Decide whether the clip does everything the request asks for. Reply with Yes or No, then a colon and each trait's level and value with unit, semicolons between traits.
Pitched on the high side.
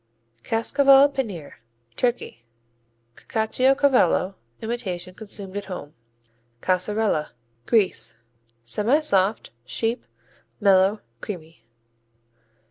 Yes: high, 205 Hz